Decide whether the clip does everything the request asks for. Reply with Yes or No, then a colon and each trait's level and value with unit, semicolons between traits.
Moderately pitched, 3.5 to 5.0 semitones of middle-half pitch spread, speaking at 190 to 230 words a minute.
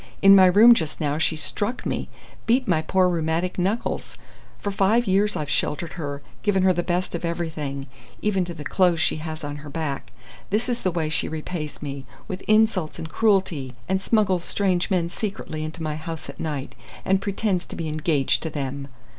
Yes: medium, 175 Hz; average, 3.8 semitones; average, 195 wpm